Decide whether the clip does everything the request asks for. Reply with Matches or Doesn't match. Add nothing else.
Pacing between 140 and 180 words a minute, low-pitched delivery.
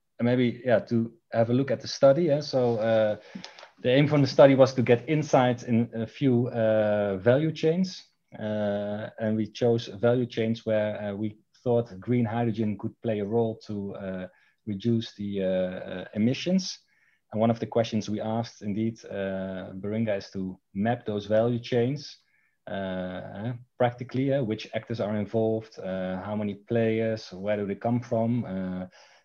Matches